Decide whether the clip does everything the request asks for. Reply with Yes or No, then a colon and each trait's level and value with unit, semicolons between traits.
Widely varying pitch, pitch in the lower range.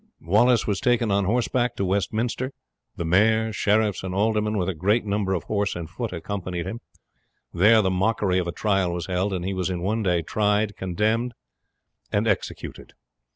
No: average, 3.1 semitones; low, 100 Hz